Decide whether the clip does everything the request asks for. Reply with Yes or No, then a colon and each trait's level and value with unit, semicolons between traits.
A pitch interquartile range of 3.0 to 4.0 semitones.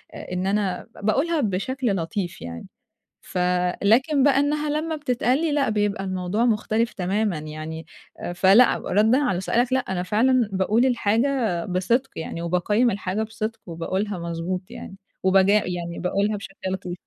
No: average, 5.2 semitones